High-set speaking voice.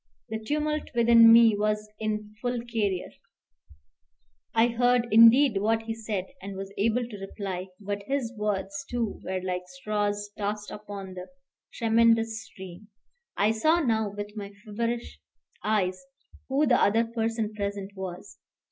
Yes: high, 215 Hz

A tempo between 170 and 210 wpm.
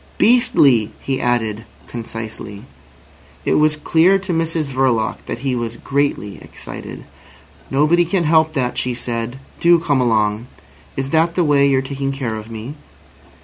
No: average, 145 wpm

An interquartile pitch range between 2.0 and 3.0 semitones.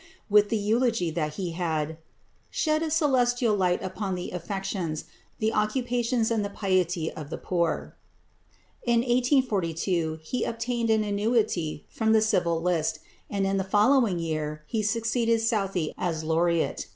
No: average, 5.3 semitones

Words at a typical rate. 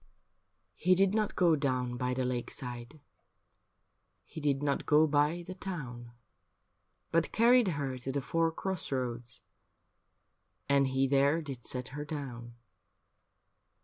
No: slow, 130 wpm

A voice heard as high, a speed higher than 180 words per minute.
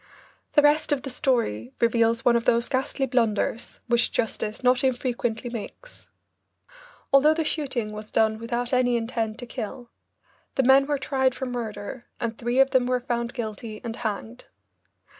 No: high, 240 Hz; average, 160 wpm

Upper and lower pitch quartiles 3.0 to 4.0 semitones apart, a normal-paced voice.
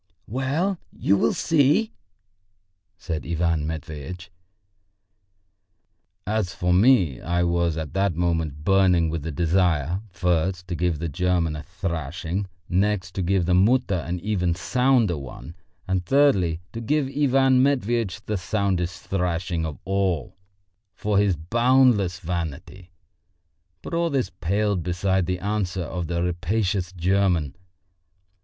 No: average, 3.5 semitones; slow, 130 wpm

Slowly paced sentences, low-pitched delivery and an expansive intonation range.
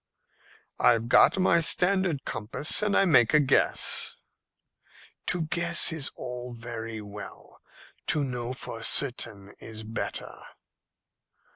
Yes: slow, 115 wpm; low, 125 Hz; wide, 6.2 semitones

